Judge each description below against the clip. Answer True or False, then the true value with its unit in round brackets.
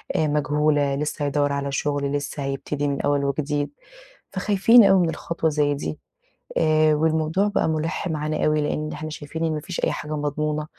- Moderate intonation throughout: False (1.5 semitones)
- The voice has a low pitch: False (150 Hz)